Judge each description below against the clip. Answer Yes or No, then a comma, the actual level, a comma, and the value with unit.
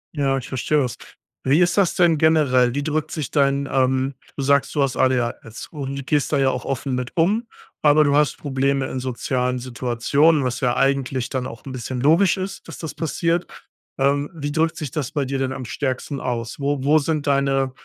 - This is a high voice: No, medium, 140 Hz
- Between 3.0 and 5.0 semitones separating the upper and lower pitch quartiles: No, narrow, 2.6 semitones